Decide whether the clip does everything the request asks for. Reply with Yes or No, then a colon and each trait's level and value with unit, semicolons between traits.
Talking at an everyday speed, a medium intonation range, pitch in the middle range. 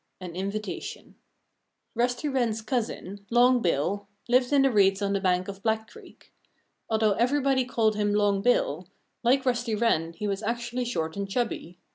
No: average, 165 wpm; average, 3.7 semitones; high, 220 Hz